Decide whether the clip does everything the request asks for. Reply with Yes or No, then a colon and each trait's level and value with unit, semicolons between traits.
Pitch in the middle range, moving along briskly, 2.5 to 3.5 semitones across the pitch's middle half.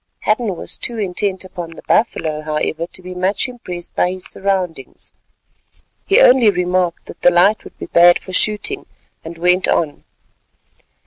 No: medium, 180 Hz; average, 155 wpm; average, 3.1 semitones